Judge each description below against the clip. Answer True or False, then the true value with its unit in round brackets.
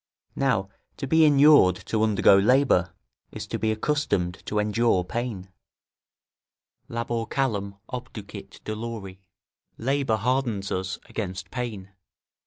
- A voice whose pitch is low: True (110 Hz)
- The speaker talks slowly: True (110 wpm)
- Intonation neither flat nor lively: True (4.4 semitones)